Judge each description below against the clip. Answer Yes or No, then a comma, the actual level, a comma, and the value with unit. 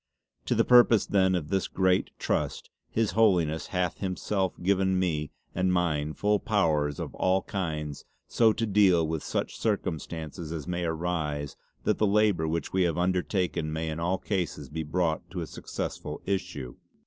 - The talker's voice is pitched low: Yes, very low, 90 Hz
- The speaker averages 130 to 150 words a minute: No, average, 170 wpm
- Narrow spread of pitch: No, average, 3.3 semitones